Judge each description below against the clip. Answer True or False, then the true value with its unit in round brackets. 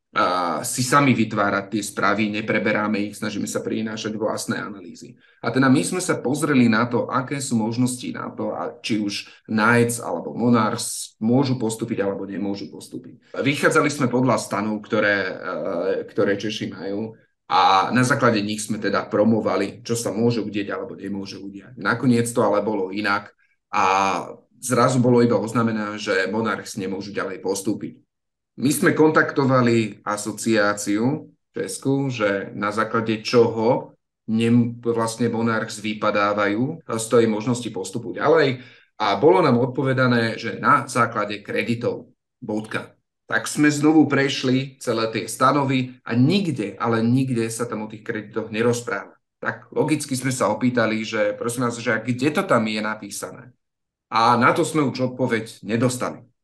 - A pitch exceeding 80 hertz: True (115 Hz)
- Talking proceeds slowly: False (150 wpm)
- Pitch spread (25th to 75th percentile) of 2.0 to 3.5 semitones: True (2.9 semitones)